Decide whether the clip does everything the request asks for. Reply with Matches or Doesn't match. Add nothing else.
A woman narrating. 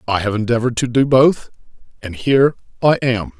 Doesn't match